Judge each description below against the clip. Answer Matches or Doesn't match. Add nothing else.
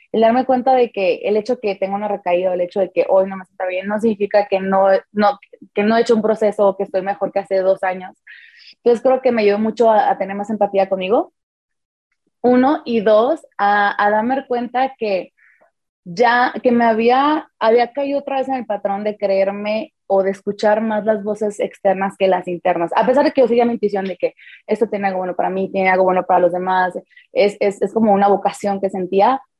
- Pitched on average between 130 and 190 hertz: Doesn't match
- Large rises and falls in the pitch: Doesn't match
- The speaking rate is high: Matches